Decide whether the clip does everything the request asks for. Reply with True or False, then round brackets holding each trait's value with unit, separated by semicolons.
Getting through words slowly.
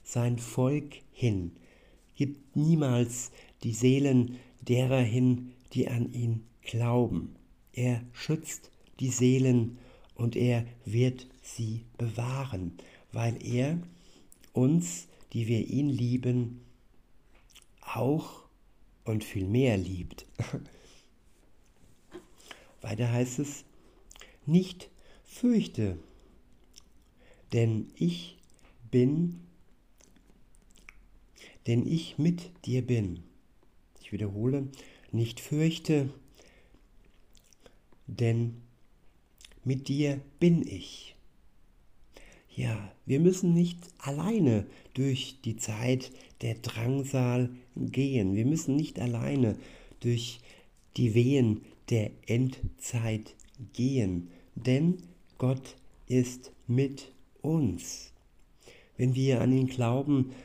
True (85 wpm)